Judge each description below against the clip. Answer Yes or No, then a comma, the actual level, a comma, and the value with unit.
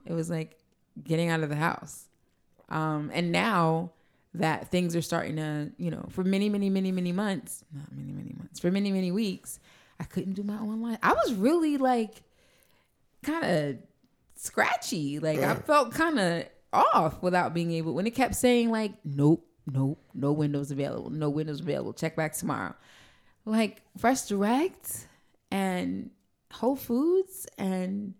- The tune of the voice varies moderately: No, wide, 5.7 semitones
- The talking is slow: No, average, 160 wpm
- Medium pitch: Yes, medium, 180 Hz